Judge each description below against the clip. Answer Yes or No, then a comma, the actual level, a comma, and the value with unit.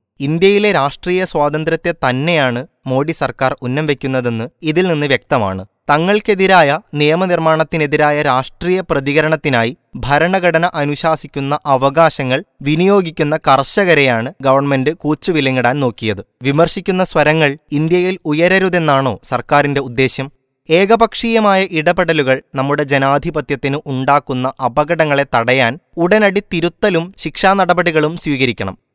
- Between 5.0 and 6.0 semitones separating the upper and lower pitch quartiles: No, average, 4.3 semitones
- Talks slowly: Yes, slow, 80 wpm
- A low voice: No, medium, 150 Hz